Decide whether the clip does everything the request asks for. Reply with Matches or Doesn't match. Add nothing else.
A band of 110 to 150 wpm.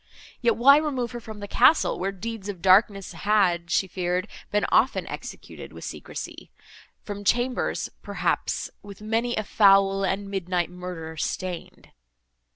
Matches